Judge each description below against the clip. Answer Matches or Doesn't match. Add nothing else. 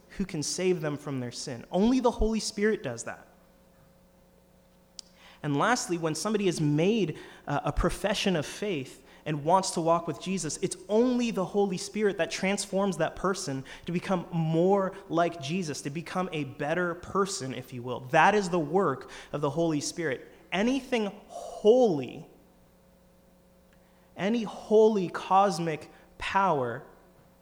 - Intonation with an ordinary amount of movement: Matches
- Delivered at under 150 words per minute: Matches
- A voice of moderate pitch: Matches